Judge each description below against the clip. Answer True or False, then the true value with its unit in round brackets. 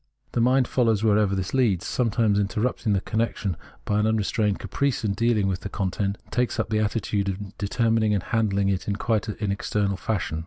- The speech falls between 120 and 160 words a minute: False (195 wpm)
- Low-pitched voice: True (105 Hz)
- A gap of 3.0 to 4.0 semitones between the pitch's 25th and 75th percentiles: False (2.4 semitones)